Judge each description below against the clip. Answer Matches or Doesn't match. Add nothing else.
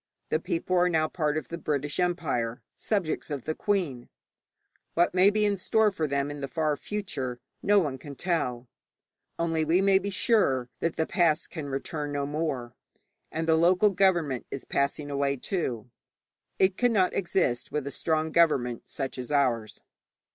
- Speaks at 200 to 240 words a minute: Doesn't match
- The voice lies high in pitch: Doesn't match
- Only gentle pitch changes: Doesn't match